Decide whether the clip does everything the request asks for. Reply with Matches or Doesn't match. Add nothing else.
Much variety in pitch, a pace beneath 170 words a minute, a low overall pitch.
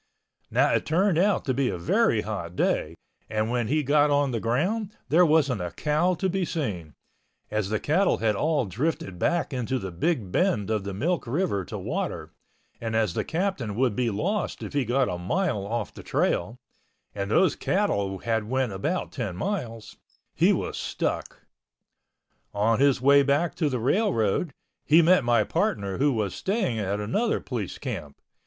Doesn't match